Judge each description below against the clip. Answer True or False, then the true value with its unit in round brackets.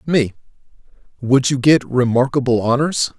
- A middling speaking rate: False (115 wpm)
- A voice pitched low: True (130 Hz)